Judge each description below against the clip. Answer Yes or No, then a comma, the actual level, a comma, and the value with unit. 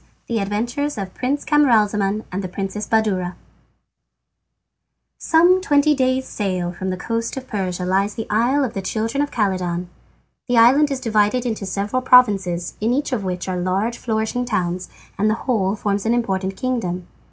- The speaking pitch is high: Yes, high, 215 Hz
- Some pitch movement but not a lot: Yes, average, 4.8 semitones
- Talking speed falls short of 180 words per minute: Yes, average, 165 wpm